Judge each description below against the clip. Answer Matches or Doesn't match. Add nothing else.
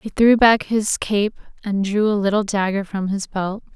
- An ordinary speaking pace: Doesn't match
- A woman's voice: Matches